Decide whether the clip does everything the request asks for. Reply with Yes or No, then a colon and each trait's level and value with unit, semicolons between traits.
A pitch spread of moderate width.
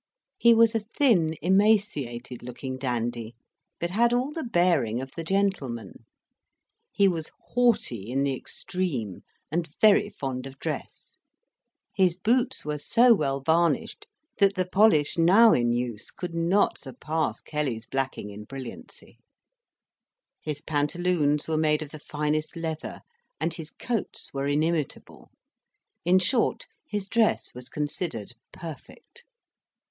No: wide, 6.6 semitones